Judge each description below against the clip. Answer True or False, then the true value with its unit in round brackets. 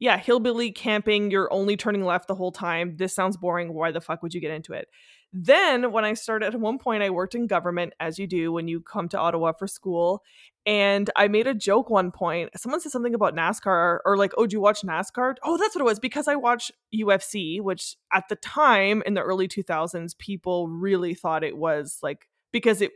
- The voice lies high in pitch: True (195 Hz)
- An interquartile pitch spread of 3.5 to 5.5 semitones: True (4.0 semitones)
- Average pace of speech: False (225 wpm)